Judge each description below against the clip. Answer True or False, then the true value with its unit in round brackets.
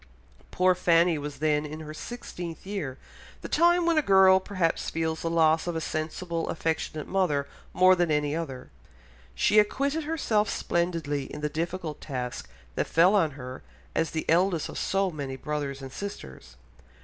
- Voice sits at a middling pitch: True (165 Hz)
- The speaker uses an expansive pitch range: False (4.0 semitones)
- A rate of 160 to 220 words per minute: True (165 wpm)